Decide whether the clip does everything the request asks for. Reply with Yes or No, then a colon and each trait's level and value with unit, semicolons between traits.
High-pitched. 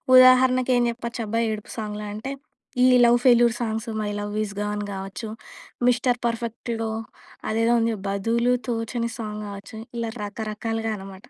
Yes: high, 225 Hz